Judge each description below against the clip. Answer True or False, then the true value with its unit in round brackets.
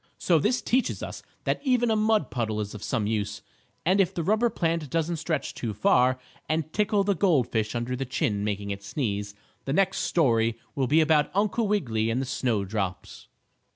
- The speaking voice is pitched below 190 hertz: True (135 Hz)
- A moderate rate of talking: True (195 wpm)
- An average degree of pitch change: False (9.0 semitones)